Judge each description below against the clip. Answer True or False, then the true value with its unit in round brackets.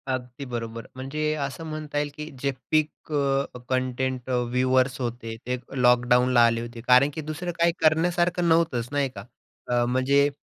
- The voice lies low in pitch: True (130 Hz)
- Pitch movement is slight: False (3.7 semitones)